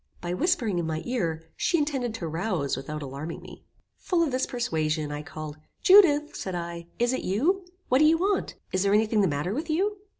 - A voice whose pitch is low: No, high, 205 Hz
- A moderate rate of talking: No, fast, 210 wpm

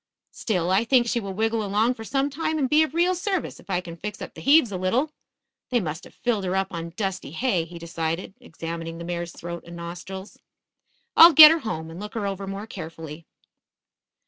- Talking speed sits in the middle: No, fast, 215 wpm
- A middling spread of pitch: No, wide, 6.3 semitones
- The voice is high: Yes, high, 195 Hz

